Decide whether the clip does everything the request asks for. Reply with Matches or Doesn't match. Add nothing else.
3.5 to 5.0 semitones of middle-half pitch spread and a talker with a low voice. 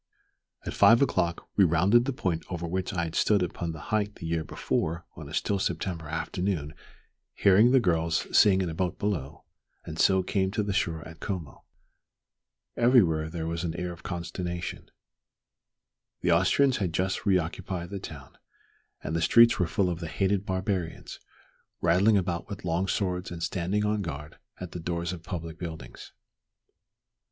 Doesn't match